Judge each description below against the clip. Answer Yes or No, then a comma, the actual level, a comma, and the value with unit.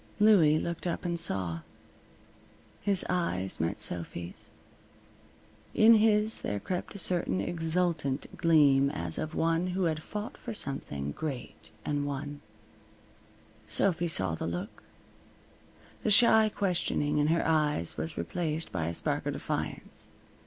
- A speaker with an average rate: No, slow, 130 wpm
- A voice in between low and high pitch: Yes, medium, 155 Hz